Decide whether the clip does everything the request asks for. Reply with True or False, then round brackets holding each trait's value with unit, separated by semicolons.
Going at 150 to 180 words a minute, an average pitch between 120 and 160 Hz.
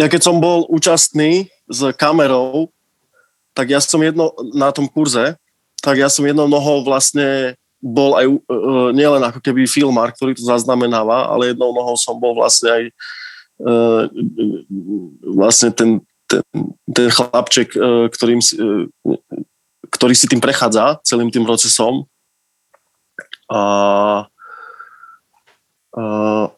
False (130 wpm; 130 Hz)